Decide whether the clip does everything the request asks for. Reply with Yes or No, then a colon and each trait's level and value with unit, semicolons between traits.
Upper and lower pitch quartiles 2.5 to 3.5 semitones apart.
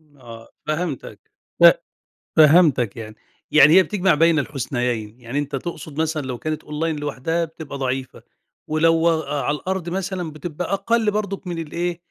No: average, 3.9 semitones